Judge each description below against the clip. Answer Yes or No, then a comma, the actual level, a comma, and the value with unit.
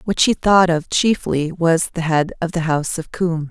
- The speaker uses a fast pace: Yes, fast, 225 wpm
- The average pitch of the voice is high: No, medium, 170 Hz